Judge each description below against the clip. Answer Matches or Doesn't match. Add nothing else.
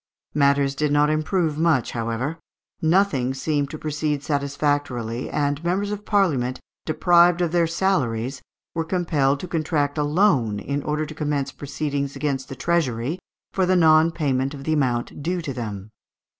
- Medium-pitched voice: Matches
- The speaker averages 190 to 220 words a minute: Doesn't match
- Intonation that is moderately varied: Matches